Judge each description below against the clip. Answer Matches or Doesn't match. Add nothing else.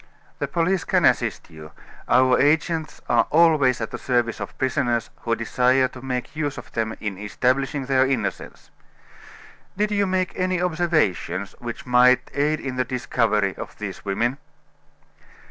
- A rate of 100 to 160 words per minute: Matches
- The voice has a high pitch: Doesn't match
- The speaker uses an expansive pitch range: Doesn't match